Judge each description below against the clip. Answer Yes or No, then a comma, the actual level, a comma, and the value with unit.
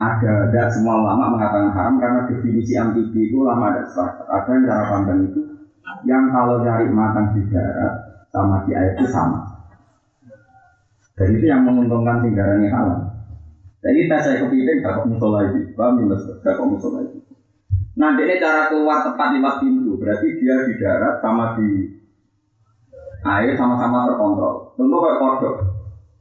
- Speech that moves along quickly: Yes, fast, 160 wpm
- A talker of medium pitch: No, low, 115 Hz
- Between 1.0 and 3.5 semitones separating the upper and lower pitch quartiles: No, average, 4.6 semitones